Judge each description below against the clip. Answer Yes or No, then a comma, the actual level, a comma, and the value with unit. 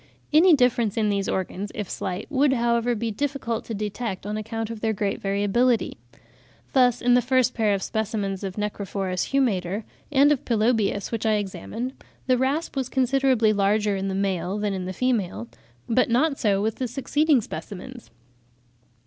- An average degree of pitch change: Yes, average, 4.0 semitones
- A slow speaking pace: No, average, 165 wpm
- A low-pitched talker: No, high, 220 Hz